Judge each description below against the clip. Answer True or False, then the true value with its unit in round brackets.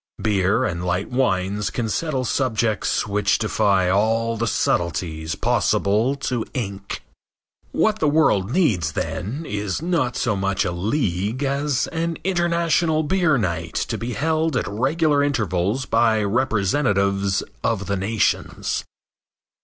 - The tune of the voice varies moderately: False (6.5 semitones)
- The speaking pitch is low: True (110 Hz)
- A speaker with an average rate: False (130 wpm)